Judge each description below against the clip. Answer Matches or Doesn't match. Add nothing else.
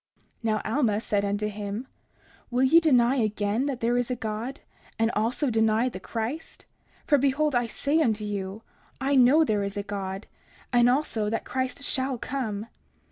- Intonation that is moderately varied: Matches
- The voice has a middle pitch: Doesn't match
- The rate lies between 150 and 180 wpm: Matches